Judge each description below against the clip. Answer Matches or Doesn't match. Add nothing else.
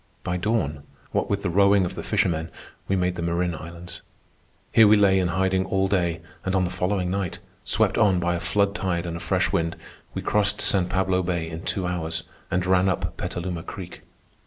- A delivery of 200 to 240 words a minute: Matches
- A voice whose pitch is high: Doesn't match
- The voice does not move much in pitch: Matches